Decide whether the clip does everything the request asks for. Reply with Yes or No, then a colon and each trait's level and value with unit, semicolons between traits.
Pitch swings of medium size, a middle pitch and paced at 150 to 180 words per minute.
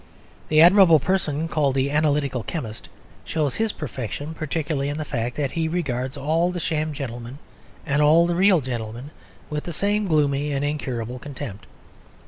Yes: average, 3.5 semitones; medium, 150 Hz; average, 160 wpm